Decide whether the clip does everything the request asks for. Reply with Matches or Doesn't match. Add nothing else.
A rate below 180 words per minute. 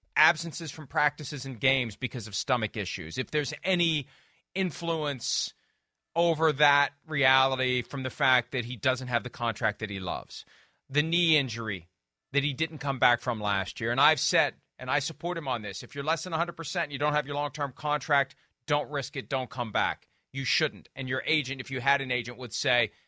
Doesn't match